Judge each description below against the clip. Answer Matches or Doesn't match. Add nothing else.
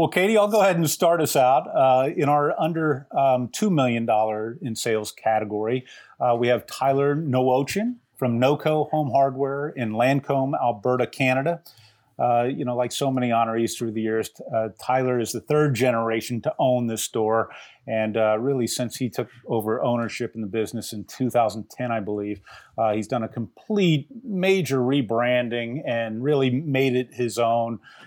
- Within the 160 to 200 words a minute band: Matches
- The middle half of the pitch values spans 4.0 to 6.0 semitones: Doesn't match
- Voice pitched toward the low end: Matches